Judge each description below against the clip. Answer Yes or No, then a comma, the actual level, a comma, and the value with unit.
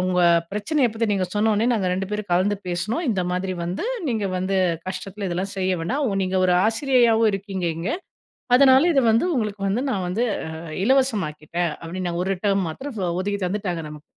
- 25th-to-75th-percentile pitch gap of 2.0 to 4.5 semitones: Yes, average, 3.5 semitones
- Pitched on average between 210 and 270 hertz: No, high, 195 Hz